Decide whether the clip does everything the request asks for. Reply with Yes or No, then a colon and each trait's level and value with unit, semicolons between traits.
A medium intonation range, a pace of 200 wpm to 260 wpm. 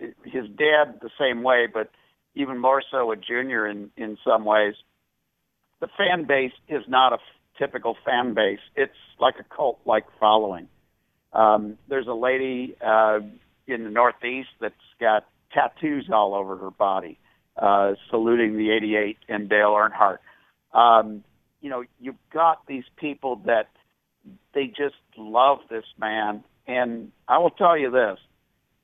No: average, 3.7 semitones; average, 150 wpm